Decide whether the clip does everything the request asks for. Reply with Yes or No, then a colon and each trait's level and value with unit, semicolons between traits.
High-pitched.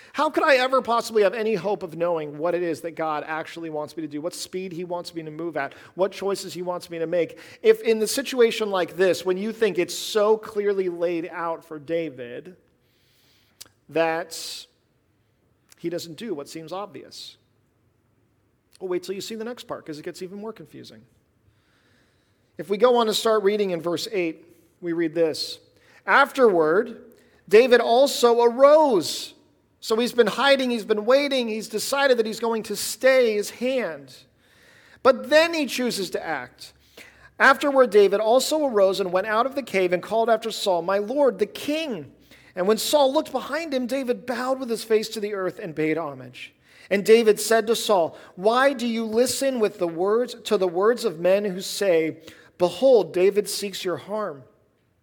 Yes: high, 200 Hz